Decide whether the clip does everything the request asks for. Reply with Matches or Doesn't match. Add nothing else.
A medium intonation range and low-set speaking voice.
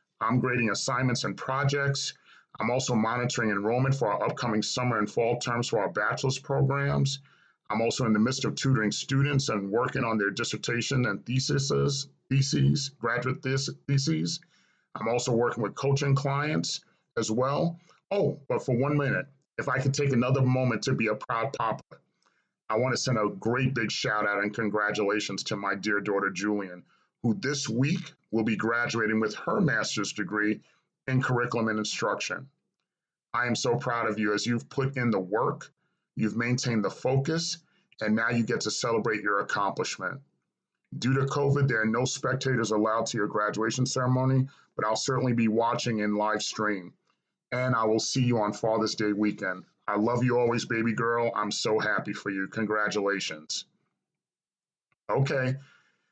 Matches